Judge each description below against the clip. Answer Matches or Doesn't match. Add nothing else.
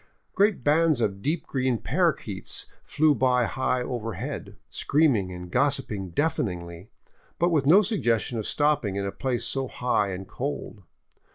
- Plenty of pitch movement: Matches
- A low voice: Matches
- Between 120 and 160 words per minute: Matches